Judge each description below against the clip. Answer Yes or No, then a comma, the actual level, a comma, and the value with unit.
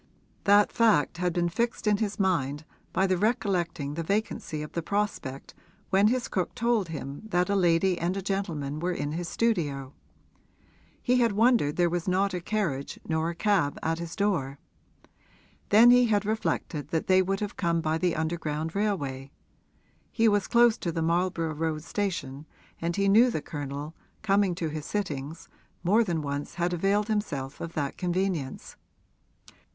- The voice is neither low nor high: Yes, medium, 175 Hz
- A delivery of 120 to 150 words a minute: No, average, 170 wpm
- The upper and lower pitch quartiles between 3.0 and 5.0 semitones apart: Yes, average, 4.6 semitones